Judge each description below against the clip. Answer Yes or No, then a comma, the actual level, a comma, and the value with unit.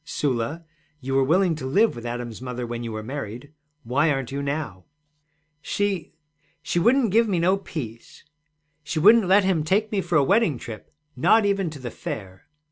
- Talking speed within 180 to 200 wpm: Yes, average, 185 wpm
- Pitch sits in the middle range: Yes, medium, 150 Hz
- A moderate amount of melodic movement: No, wide, 7.6 semitones